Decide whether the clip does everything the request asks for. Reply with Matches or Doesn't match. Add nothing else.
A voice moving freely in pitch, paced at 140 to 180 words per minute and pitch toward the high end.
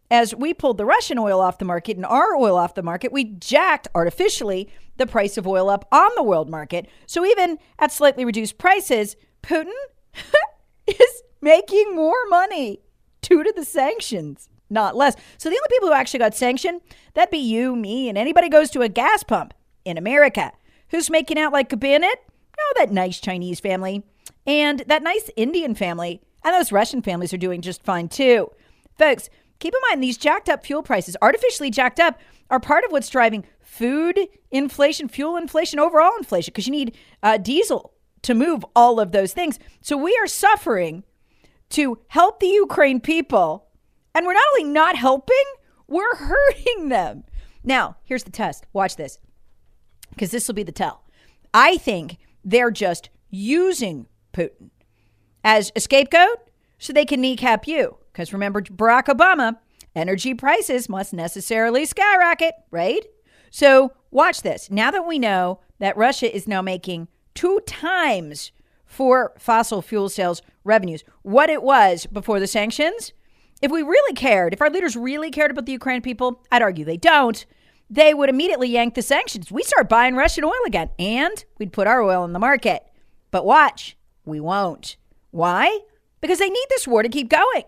Matches